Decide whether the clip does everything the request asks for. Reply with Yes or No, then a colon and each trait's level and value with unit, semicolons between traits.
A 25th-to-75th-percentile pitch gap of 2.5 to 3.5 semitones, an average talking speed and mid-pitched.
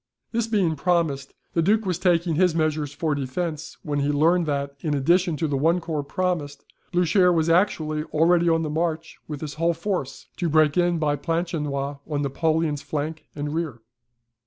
Yes: average, 2.8 semitones; average, 180 wpm; medium, 160 Hz